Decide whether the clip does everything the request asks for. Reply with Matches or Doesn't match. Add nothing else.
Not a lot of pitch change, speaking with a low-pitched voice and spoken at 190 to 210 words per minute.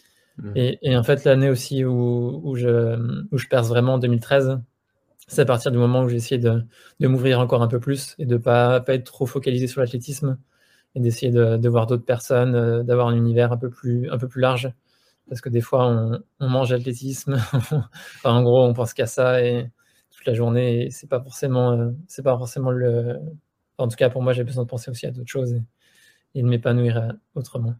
Doesn't match